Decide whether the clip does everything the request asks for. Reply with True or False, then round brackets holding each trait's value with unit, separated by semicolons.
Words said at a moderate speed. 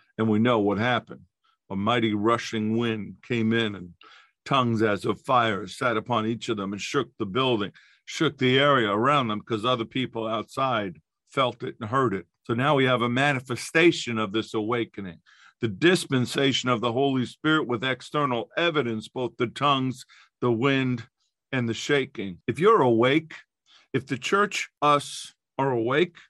True (170 wpm)